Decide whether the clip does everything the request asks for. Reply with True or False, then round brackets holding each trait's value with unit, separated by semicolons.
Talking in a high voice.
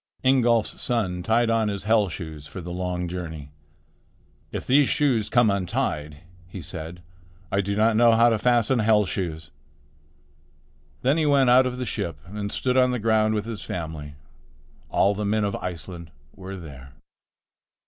False (105 Hz)